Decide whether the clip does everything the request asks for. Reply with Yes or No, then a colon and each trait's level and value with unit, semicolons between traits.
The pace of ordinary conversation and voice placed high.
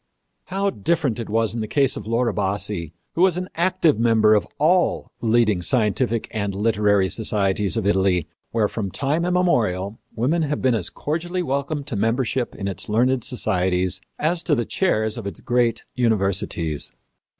No: average, 170 wpm; low, 115 Hz